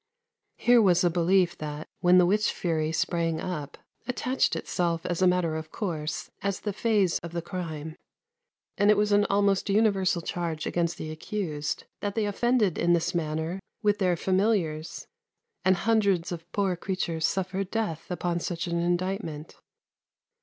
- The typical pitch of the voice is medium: Yes, medium, 180 Hz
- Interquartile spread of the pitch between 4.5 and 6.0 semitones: No, average, 3.2 semitones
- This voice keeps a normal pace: Yes, average, 160 wpm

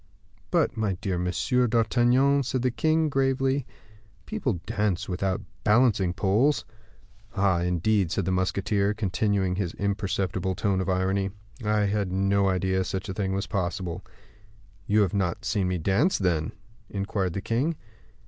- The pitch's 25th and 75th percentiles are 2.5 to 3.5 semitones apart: Yes, average, 3.2 semitones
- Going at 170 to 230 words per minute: No, average, 145 wpm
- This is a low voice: Yes, low, 100 Hz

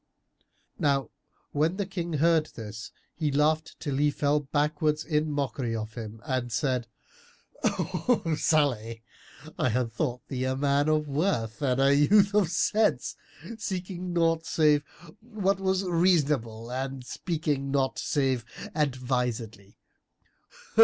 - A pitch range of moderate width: Yes, average, 4.5 semitones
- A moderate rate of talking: No, slow, 125 wpm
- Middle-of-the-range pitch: Yes, medium, 145 Hz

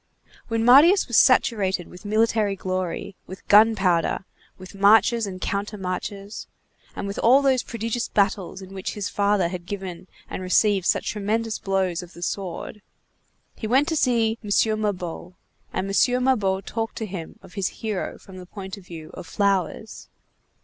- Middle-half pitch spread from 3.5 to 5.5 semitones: No, average, 3.1 semitones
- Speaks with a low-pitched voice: No, high, 200 Hz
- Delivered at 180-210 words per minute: No, average, 160 wpm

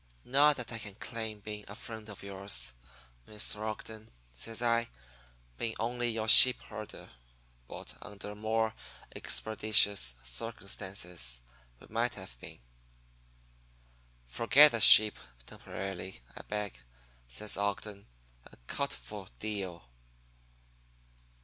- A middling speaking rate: No, slow, 110 wpm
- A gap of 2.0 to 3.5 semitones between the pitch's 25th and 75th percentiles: Yes, narrow, 2.6 semitones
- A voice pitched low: Yes, low, 105 Hz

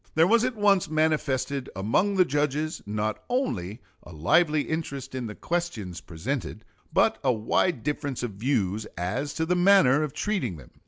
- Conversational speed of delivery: Yes, average, 165 wpm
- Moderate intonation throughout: No, wide, 7.4 semitones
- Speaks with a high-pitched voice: No, medium, 140 Hz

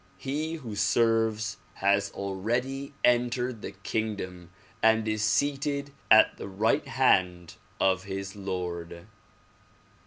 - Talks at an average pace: No, slow, 105 wpm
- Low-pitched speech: Yes, low, 110 Hz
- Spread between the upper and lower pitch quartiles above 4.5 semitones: No, average, 4.2 semitones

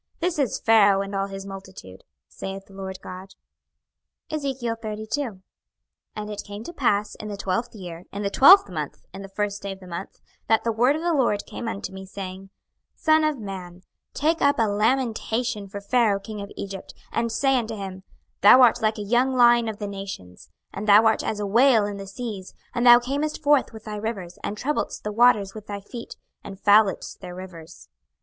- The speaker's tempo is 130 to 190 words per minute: No, average, 200 wpm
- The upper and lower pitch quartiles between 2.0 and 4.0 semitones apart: Yes, average, 3.6 semitones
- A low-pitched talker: No, high, 210 Hz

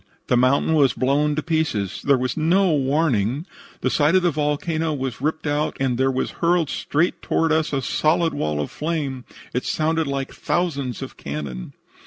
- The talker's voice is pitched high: No, medium, 145 Hz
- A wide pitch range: No, average, 3.6 semitones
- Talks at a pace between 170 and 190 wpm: Yes, average, 180 wpm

